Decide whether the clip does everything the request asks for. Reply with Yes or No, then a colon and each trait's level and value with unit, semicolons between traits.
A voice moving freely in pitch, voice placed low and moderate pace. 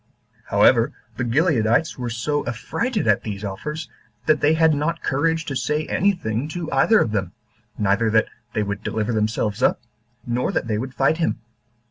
Yes: wide, 6.4 semitones; low, 125 Hz; average, 175 wpm